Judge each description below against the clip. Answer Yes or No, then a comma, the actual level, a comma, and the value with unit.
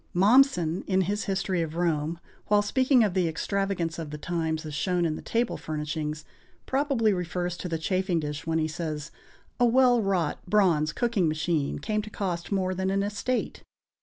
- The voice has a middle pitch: Yes, medium, 180 Hz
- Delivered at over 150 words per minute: Yes, average, 180 wpm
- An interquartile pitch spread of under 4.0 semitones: No, average, 4.3 semitones